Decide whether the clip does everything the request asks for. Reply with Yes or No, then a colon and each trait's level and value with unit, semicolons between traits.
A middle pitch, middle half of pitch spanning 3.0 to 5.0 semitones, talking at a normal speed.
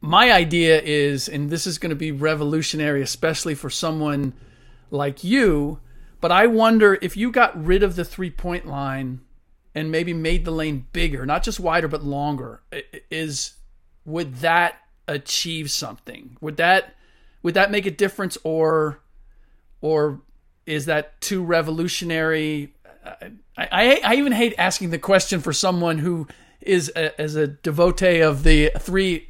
Yes: medium, 160 Hz; average, 3.3 semitones; average, 150 wpm